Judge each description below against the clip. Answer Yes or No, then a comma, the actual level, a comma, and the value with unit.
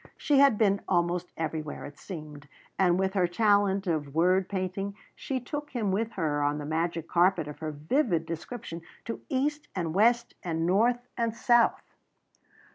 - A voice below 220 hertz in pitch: Yes, medium, 185 Hz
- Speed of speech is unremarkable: Yes, average, 165 wpm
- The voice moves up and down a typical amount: No, wide, 5.8 semitones